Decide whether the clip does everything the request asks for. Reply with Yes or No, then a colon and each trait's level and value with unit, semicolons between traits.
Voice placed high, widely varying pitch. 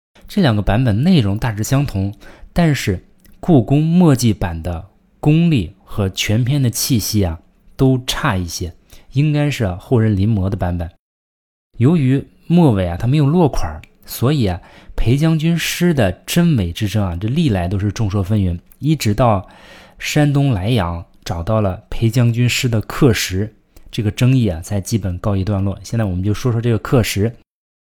No: low, 110 Hz; wide, 5.8 semitones